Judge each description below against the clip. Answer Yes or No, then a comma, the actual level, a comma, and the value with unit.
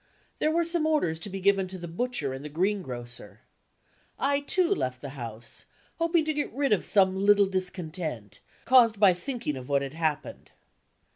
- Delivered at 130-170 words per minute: No, average, 185 wpm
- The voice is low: No, high, 190 Hz